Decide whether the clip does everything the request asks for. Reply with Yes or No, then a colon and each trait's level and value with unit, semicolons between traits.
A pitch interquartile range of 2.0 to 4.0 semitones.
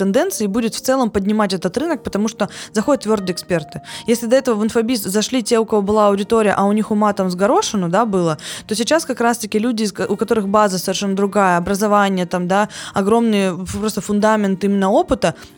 Yes: average, 2.8 semitones